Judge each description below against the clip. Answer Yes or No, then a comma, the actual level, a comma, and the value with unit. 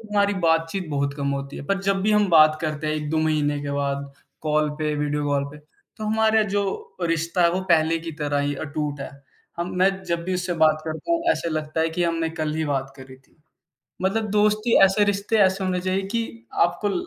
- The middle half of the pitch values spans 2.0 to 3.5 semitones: No, average, 4.6 semitones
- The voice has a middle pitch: Yes, medium, 165 Hz